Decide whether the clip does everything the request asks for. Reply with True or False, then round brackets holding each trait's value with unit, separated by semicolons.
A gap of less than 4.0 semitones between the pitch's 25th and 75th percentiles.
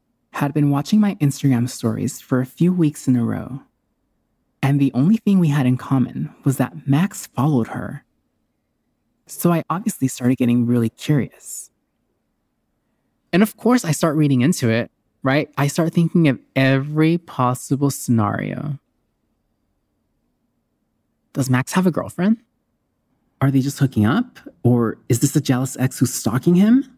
False (4.7 semitones)